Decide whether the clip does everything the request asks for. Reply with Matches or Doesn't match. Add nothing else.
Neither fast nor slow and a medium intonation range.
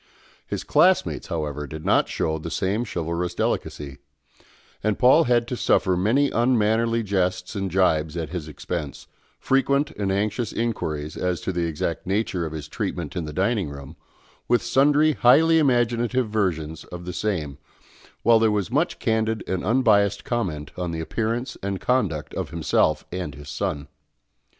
Doesn't match